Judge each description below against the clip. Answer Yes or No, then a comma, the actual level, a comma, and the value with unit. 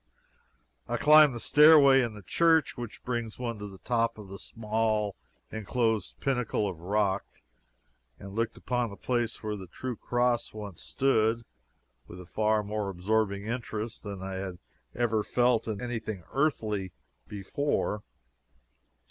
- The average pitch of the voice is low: Yes, low, 110 Hz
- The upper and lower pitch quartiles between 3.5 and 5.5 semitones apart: No, average, 3.1 semitones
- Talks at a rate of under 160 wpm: Yes, average, 150 wpm